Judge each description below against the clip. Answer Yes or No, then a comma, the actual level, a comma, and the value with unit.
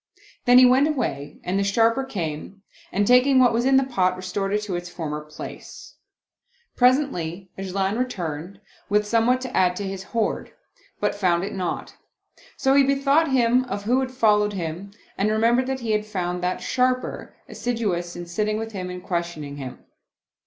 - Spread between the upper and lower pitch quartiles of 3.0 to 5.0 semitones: No, wide, 5.6 semitones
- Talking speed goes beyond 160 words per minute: Yes, average, 180 wpm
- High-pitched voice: Yes, high, 210 Hz